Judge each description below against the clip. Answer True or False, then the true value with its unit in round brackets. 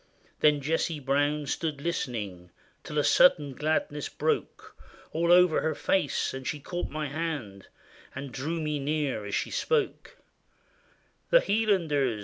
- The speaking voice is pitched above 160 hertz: False (150 Hz)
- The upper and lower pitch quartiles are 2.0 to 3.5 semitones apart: True (3.2 semitones)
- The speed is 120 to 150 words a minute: True (145 wpm)